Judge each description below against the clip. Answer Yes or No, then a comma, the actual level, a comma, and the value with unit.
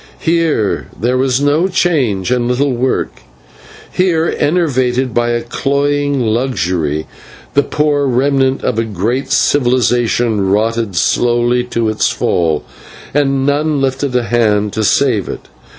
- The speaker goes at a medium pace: No, slow, 130 wpm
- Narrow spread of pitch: No, average, 3.9 semitones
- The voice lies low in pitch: Yes, low, 125 Hz